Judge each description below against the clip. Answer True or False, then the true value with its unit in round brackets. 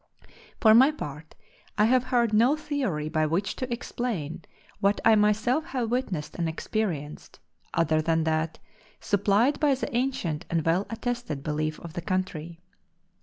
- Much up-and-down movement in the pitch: True (7.2 semitones)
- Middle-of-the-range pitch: False (200 Hz)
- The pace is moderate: True (150 wpm)